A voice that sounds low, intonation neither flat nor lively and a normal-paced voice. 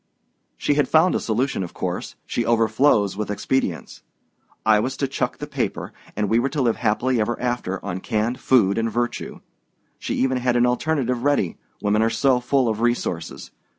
Yes: low, 120 Hz; average, 3.4 semitones; average, 185 wpm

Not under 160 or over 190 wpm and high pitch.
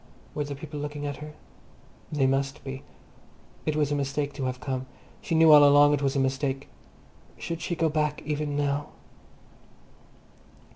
No: average, 165 wpm; medium, 145 Hz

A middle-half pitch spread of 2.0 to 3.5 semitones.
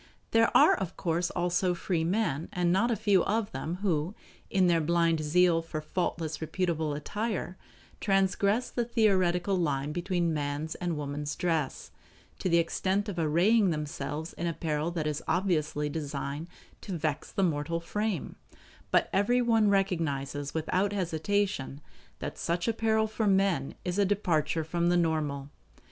No: average, 4.0 semitones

